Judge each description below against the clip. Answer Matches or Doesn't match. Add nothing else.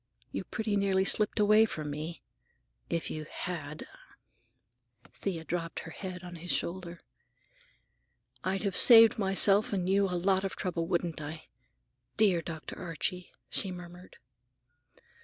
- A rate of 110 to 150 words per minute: Matches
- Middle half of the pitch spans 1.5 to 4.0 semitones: Matches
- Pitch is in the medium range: Matches